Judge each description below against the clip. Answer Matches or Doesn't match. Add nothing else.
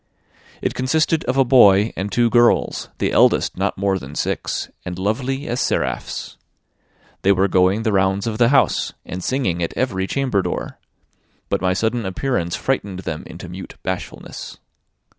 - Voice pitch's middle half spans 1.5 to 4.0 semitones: Doesn't match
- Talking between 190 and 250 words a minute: Doesn't match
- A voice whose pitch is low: Matches